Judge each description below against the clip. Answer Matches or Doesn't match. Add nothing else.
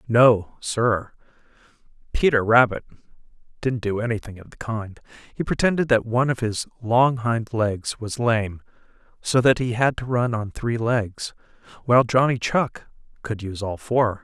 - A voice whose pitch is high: Doesn't match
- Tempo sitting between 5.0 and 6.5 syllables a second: Doesn't match